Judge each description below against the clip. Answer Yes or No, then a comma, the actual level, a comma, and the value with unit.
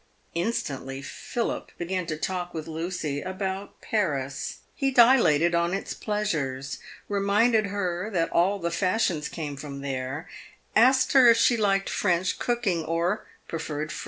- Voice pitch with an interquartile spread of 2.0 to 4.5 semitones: No, average, 5.1 semitones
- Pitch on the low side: No, medium, 180 Hz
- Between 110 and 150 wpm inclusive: Yes, average, 140 wpm